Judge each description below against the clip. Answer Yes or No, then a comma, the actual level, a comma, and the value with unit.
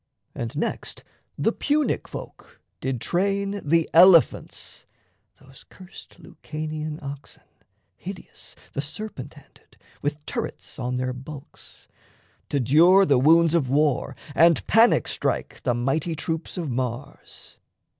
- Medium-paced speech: No, slow, 120 wpm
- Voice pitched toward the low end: No, medium, 155 Hz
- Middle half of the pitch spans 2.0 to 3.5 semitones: No, average, 4.1 semitones